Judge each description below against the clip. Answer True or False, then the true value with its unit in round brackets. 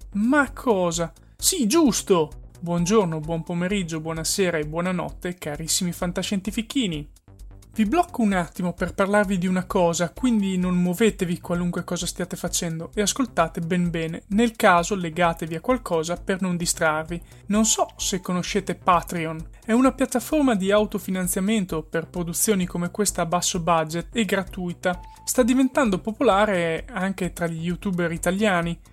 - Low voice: False (180 Hz)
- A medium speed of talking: True (140 wpm)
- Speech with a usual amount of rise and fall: True (3.6 semitones)